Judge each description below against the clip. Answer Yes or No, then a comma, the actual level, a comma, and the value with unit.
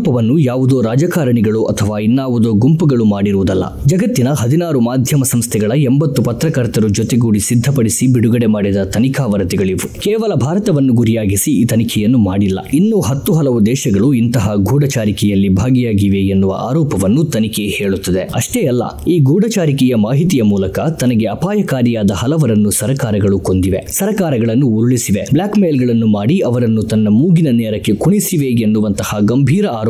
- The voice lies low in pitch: Yes, low, 120 Hz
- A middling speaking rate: No, fast, 120 wpm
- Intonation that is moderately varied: Yes, average, 5.0 semitones